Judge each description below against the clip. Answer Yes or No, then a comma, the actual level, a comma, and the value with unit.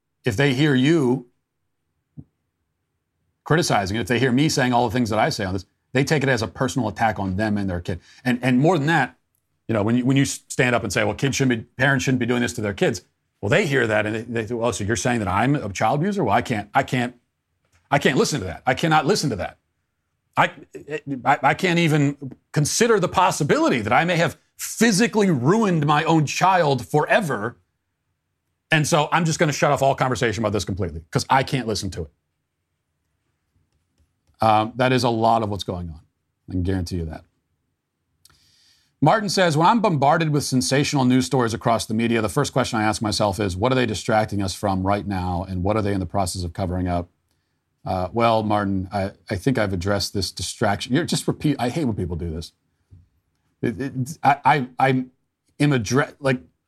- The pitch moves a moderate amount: No, wide, 5.8 semitones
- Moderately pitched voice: No, low, 120 Hz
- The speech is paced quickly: Yes, fast, 215 wpm